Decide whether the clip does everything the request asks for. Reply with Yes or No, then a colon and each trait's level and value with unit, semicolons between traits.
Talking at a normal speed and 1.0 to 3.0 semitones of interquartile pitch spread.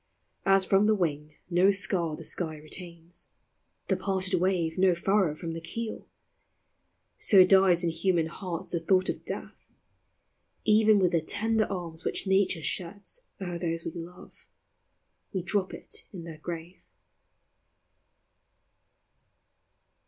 No: slow, 130 wpm; narrow, 2.6 semitones